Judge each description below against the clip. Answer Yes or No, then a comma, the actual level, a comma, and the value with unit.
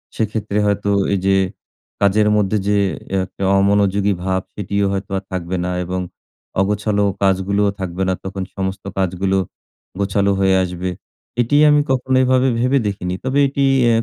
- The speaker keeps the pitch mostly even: Yes, narrow, 1.8 semitones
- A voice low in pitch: Yes, low, 100 Hz